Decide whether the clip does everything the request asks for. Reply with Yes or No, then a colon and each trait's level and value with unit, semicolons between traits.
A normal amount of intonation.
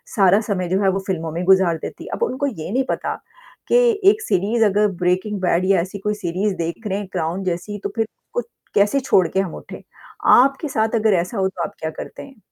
Yes: average, 3.3 semitones